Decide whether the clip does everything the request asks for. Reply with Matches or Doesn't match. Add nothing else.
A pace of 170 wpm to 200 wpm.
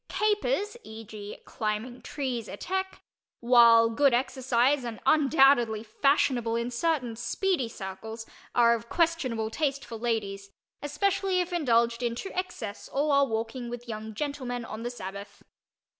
Doesn't match